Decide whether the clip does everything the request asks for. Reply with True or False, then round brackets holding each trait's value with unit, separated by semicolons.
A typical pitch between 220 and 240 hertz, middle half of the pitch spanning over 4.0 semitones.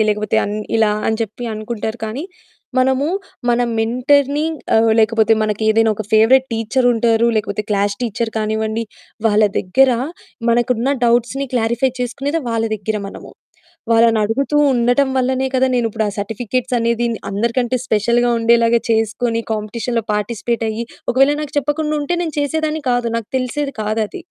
False (235 Hz; 2.8 semitones)